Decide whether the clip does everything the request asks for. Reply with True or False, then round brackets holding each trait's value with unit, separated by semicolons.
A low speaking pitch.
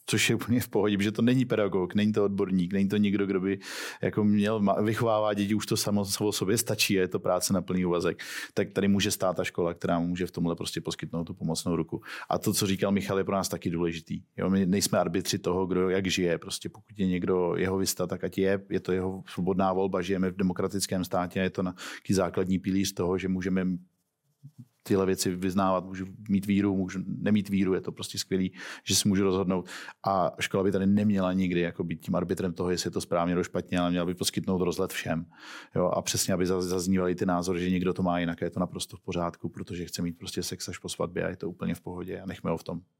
True (95 Hz)